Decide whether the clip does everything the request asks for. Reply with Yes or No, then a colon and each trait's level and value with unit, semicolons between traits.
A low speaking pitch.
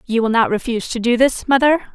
No: high, 245 Hz